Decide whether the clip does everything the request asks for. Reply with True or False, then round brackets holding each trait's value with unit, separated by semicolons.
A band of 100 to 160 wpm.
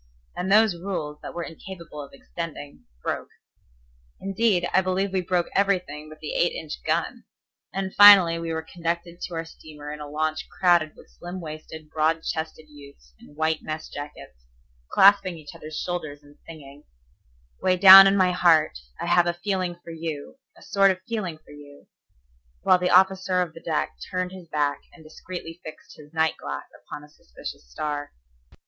False (175 wpm)